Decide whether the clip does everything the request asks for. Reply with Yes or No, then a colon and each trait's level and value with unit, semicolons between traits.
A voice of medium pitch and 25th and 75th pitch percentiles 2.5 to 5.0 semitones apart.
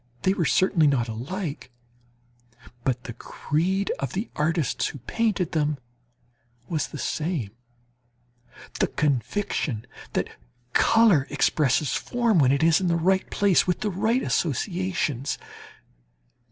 No: medium, 160 Hz; wide, 5.4 semitones